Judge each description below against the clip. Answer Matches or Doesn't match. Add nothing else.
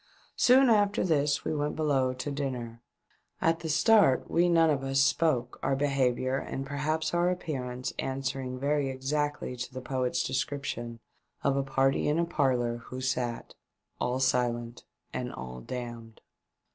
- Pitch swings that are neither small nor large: Matches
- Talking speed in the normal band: Matches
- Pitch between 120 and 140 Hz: Matches